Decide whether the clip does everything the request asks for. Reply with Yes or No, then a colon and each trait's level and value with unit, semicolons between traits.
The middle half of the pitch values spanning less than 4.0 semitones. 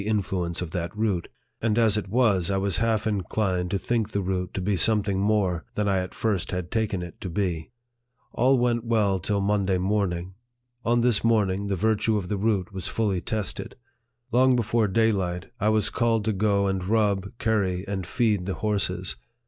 Yes: average, 2.9 semitones